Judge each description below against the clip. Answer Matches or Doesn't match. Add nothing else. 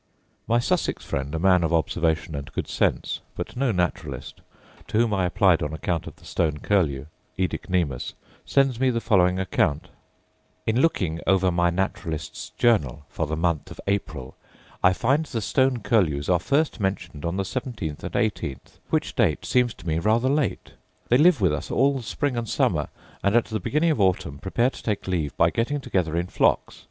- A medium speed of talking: Matches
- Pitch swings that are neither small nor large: Doesn't match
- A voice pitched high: Doesn't match